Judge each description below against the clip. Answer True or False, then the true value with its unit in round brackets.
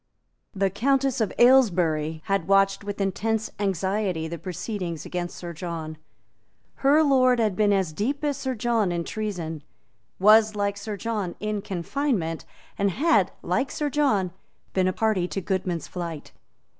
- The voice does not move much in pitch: False (4.2 semitones)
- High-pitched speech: True (200 Hz)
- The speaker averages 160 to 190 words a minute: False (150 wpm)